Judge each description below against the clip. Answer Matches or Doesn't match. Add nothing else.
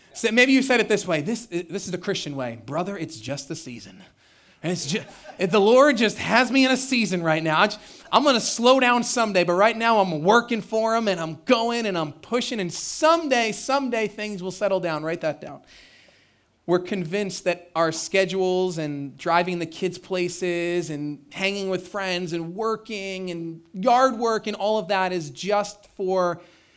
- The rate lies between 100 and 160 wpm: Doesn't match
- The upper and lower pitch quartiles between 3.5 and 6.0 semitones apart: Matches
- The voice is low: Doesn't match